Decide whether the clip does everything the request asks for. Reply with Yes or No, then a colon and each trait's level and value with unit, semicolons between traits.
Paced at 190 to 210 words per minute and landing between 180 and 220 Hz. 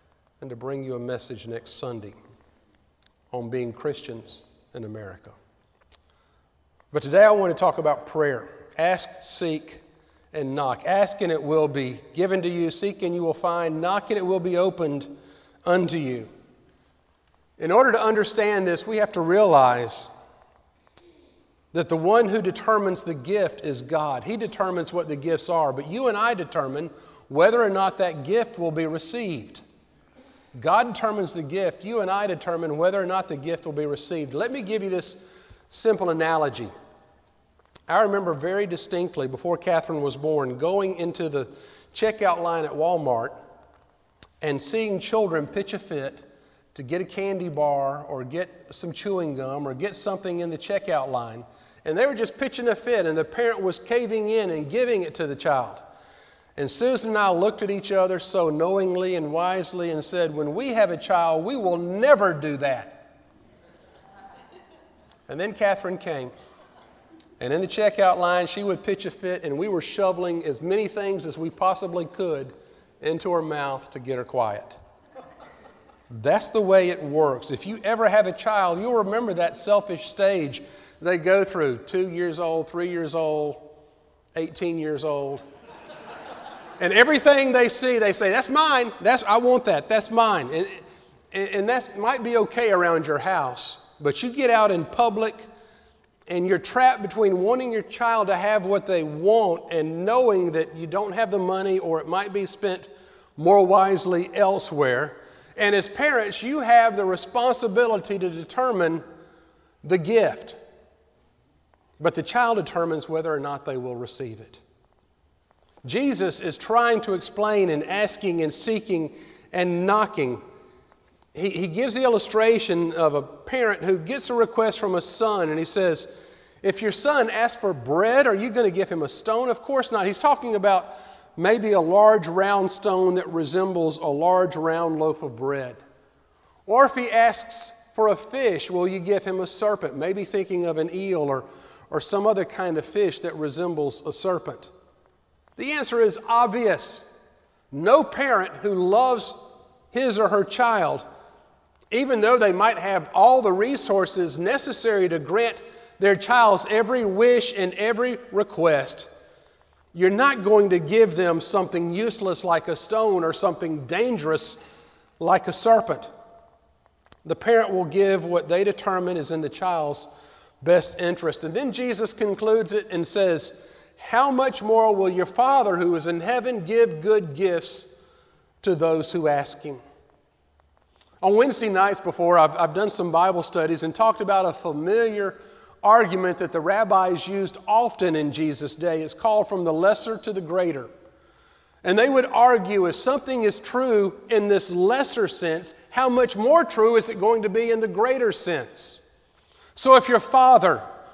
No: average, 170 wpm; medium, 185 Hz